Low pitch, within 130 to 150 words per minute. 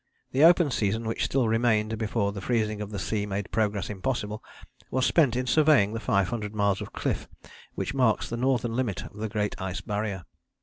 No: low, 110 Hz; average, 190 wpm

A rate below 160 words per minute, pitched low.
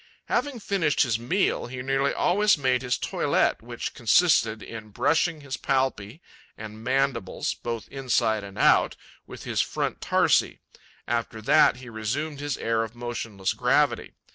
Yes: average, 145 wpm; low, 125 Hz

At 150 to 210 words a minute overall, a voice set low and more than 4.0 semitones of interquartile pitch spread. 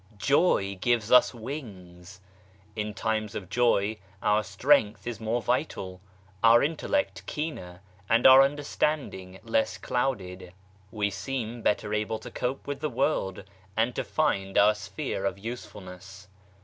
No: slow, 135 wpm; low, 110 Hz; average, 4.5 semitones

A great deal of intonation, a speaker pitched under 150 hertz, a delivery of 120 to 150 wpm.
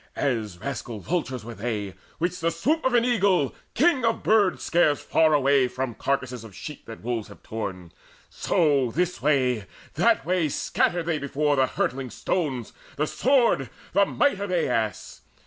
No: wide, 6.7 semitones; medium, 140 Hz; average, 165 wpm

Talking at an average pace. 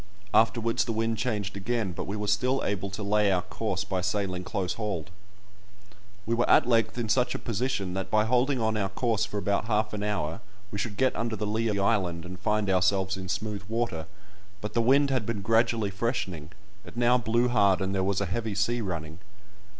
No: fast, 210 wpm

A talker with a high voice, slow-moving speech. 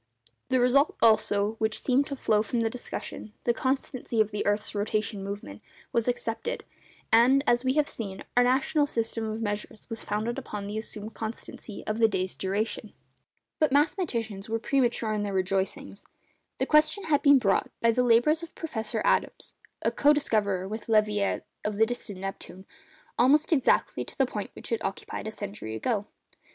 No: high, 225 Hz; average, 165 wpm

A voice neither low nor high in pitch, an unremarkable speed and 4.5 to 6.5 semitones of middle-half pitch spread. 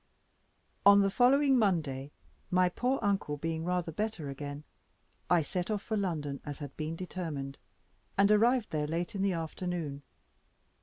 Yes: medium, 175 Hz; average, 150 wpm; average, 5.1 semitones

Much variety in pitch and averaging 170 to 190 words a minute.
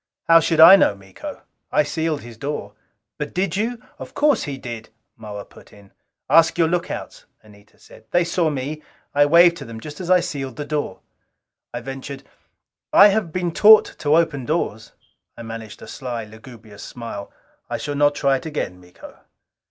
Yes: wide, 6.7 semitones; average, 180 wpm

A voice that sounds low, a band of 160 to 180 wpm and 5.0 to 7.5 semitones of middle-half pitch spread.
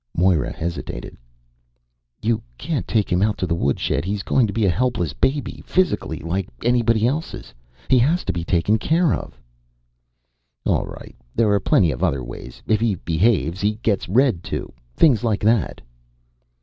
Yes: low, 105 Hz; average, 165 wpm; wide, 5.6 semitones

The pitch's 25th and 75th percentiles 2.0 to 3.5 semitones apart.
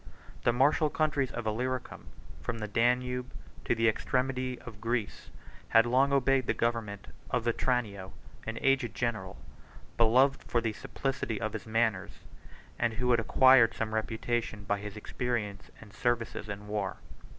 Yes: average, 2.7 semitones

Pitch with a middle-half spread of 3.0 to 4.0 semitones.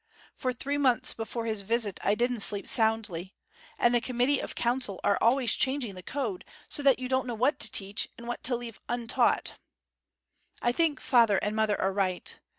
Yes: average, 3.5 semitones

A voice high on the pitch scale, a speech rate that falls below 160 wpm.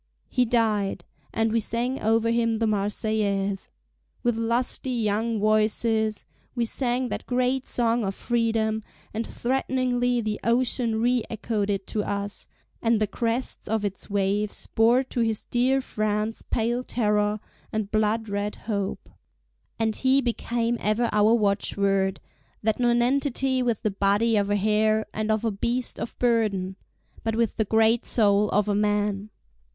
Yes: high, 220 Hz; average, 145 wpm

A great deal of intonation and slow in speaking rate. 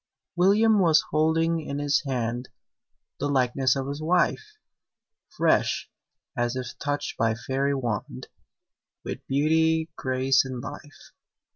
No: average, 3.8 semitones; slow, 120 wpm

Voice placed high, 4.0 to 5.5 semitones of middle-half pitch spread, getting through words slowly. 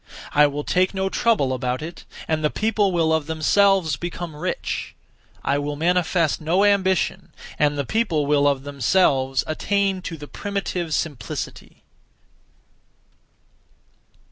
No: medium, 160 Hz; average, 4.6 semitones; slow, 130 wpm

